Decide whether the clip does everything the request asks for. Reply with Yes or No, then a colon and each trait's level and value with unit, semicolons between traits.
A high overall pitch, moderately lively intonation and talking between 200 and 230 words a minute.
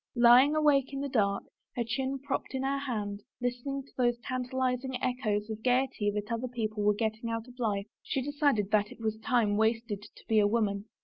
Yes: high, 235 Hz; average, 3.5 semitones; fast, 205 wpm